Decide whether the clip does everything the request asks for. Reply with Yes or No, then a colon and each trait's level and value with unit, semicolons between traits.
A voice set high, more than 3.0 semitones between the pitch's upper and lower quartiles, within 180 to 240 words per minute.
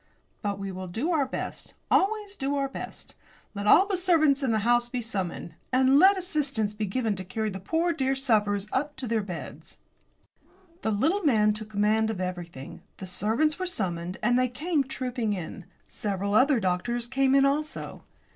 Yes: high, 240 Hz; wide, 5.6 semitones; average, 185 wpm